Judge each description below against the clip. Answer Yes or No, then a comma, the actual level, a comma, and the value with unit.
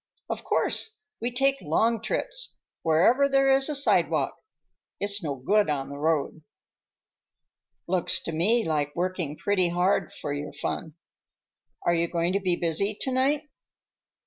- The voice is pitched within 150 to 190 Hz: Yes, medium, 185 Hz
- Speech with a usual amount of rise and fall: No, wide, 7.7 semitones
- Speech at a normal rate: Yes, average, 145 wpm